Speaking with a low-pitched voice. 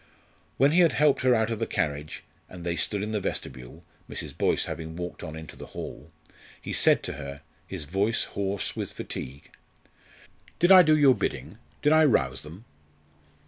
Yes: low, 100 Hz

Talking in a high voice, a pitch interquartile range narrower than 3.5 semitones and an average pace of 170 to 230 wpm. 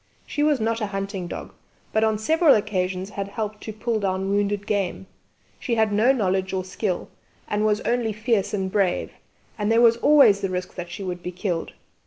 Yes: high, 205 Hz; average, 2.7 semitones; average, 200 wpm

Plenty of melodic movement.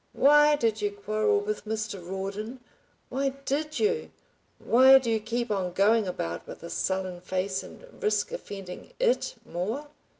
Yes: wide, 7.0 semitones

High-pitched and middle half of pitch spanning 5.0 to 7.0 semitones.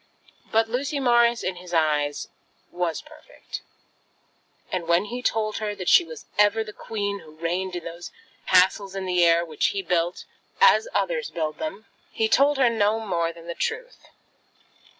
Yes: high, 200 Hz; wide, 5.5 semitones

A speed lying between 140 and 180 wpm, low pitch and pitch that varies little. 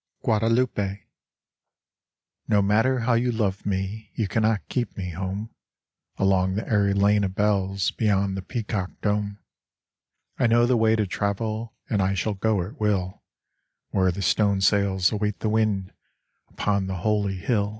Yes: average, 150 wpm; low, 100 Hz; narrow, 2.2 semitones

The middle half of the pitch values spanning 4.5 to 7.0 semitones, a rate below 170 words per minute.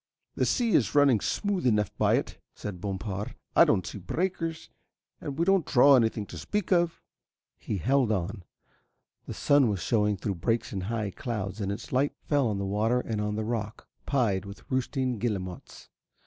No: wide, 5.5 semitones; average, 180 wpm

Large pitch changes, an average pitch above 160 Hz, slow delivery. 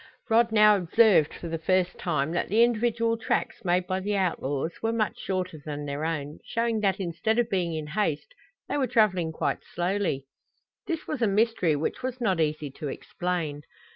No: wide, 5.7 semitones; medium, 185 Hz; average, 185 wpm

